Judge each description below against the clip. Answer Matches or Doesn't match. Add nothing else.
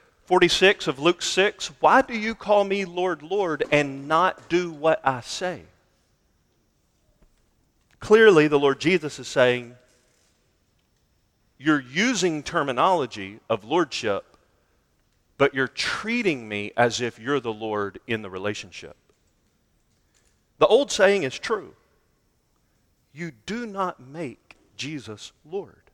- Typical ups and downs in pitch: Doesn't match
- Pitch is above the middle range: Doesn't match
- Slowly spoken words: Matches